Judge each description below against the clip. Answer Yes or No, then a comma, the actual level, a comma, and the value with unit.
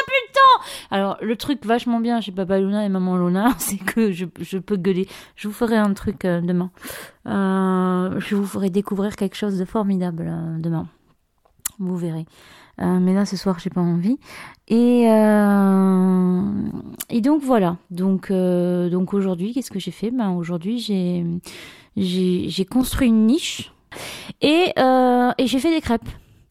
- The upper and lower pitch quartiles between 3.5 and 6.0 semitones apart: Yes, average, 4.0 semitones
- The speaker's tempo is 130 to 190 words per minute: Yes, average, 155 wpm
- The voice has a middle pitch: No, high, 195 Hz